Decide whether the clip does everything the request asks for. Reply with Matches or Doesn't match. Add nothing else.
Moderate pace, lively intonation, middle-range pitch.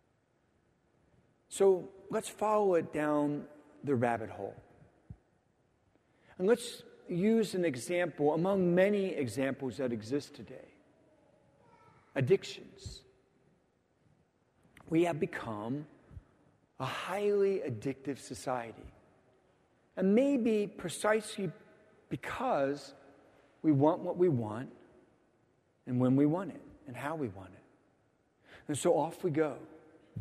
Doesn't match